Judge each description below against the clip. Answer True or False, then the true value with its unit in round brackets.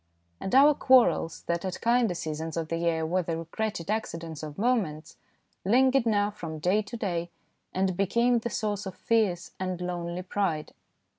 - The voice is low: False (185 Hz)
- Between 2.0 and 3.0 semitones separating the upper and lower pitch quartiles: False (4.8 semitones)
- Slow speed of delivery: False (170 wpm)